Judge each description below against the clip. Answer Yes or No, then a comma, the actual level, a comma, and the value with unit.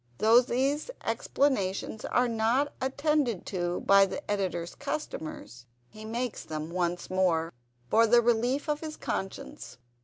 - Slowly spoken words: Yes, slow, 130 wpm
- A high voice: Yes, high, 220 Hz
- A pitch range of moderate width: No, wide, 6.3 semitones